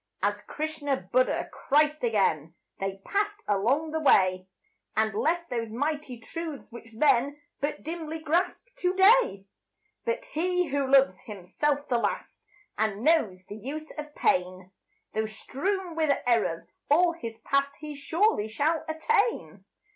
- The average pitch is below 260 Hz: No, very high, 285 Hz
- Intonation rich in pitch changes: Yes, wide, 6.8 semitones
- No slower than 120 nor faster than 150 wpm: Yes, average, 140 wpm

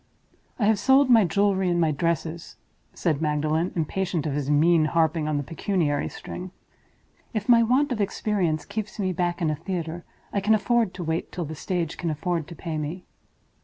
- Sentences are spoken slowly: No, average, 190 wpm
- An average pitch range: Yes, average, 4.1 semitones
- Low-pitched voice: No, medium, 175 Hz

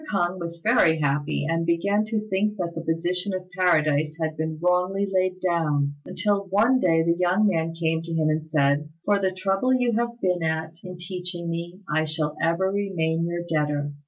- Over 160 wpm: Yes, average, 190 wpm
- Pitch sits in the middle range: Yes, medium, 170 Hz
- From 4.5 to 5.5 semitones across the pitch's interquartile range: No, average, 3.0 semitones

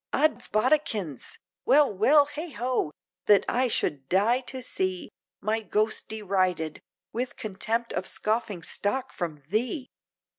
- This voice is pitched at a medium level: No, high, 220 Hz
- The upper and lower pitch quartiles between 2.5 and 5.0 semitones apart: No, wide, 5.4 semitones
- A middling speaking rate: No, slow, 115 wpm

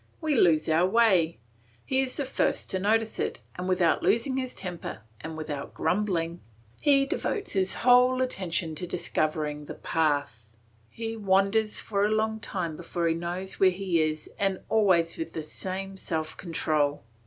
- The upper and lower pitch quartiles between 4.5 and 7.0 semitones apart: Yes, average, 5.1 semitones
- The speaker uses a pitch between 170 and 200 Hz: Yes, medium, 185 Hz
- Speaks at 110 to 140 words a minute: No, average, 165 wpm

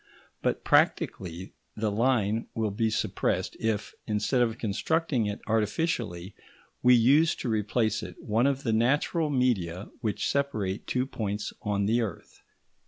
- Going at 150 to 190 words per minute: No, average, 140 wpm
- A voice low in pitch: Yes, low, 110 Hz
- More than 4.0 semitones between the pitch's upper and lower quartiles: No, average, 3.5 semitones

